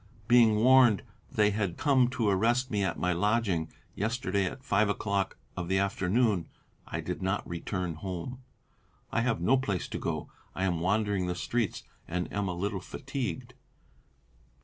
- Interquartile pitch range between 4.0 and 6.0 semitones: Yes, average, 4.5 semitones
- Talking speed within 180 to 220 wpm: No, average, 165 wpm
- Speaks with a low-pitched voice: Yes, low, 100 Hz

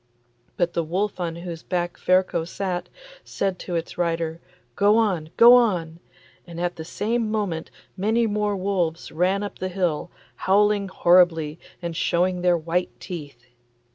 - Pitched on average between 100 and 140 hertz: No, medium, 180 Hz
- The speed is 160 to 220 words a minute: No, average, 150 wpm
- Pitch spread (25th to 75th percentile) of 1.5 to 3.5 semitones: Yes, average, 2.9 semitones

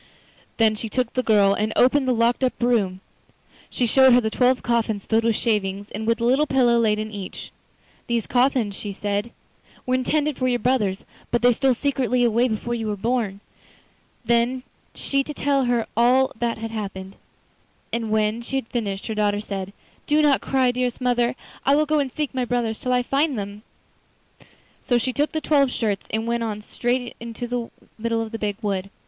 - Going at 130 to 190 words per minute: No, average, 200 wpm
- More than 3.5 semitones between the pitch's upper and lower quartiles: No, average, 2.9 semitones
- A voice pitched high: Yes, high, 235 Hz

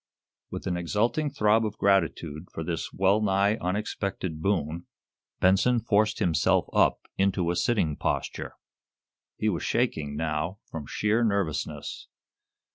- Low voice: Yes, very low, 95 Hz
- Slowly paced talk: Yes, slow, 125 wpm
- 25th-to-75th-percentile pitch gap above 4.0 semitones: Yes, average, 4.6 semitones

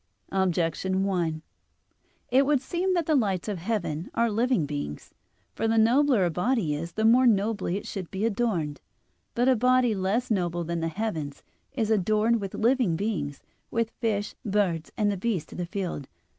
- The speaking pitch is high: Yes, high, 205 Hz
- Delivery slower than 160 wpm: No, average, 175 wpm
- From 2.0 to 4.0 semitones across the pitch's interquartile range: No, average, 5.1 semitones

